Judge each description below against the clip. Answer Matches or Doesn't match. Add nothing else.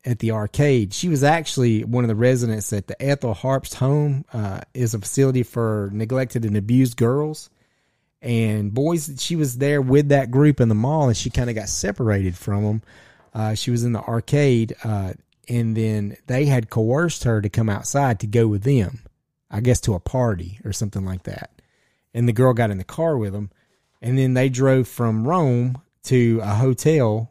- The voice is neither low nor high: Doesn't match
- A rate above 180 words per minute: Matches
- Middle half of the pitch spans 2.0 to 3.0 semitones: Doesn't match